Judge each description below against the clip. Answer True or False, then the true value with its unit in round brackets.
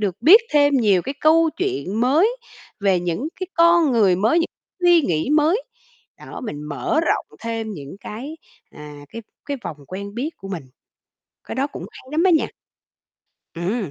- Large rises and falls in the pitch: True (9.0 semitones)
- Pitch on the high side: True (240 Hz)